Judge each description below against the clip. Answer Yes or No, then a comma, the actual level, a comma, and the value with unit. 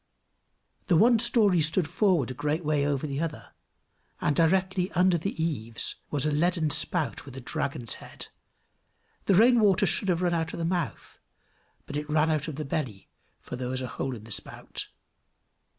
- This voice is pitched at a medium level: Yes, medium, 160 Hz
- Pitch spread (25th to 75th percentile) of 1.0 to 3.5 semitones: No, average, 4.3 semitones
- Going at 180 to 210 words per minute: Yes, average, 185 wpm